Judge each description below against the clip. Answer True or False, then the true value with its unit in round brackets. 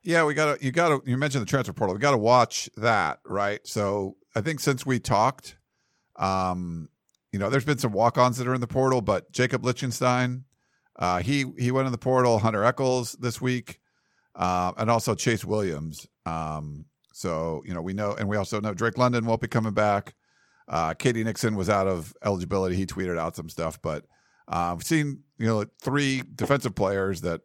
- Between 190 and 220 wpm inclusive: True (205 wpm)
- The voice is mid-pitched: False (115 Hz)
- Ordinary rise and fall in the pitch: True (5.0 semitones)